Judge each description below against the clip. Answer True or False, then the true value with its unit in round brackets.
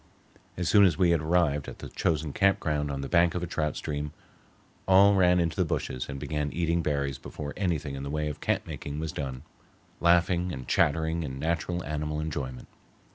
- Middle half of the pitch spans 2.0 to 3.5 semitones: True (3.1 semitones)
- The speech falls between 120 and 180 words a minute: False (195 wpm)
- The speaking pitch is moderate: False (75 Hz)